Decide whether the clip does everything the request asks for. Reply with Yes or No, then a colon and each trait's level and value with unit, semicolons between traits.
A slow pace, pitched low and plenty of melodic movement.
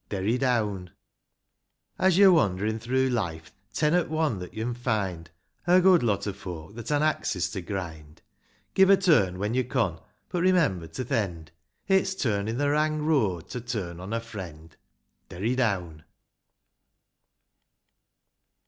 No: average, 150 wpm; low, 110 Hz; wide, 8.2 semitones